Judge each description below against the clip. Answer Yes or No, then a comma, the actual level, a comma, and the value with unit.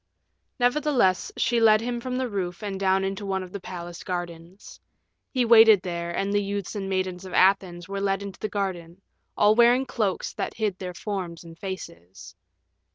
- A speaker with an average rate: Yes, average, 180 wpm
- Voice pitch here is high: Yes, high, 195 Hz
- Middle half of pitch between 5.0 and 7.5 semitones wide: No, average, 3.1 semitones